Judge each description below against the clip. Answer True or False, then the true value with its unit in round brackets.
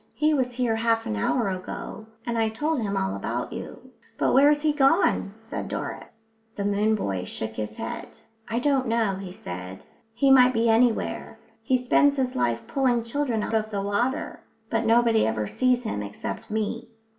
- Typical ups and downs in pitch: True (4.2 semitones)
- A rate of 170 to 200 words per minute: True (180 wpm)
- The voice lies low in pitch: False (225 Hz)